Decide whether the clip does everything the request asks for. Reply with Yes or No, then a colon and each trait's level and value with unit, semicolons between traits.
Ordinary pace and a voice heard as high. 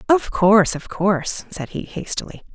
Yes: average, 165 wpm; high, 195 Hz